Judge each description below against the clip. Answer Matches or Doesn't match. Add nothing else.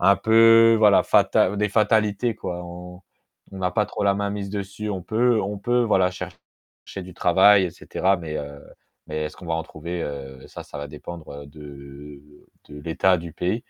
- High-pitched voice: Doesn't match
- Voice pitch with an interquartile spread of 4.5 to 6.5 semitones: Matches